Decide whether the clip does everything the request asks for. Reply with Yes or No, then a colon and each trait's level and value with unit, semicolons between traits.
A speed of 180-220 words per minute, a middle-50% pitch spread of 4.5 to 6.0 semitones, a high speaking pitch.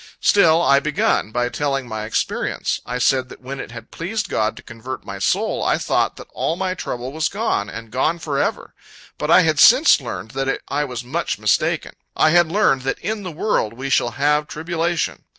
No: average, 200 wpm; wide, 5.4 semitones; medium, 140 Hz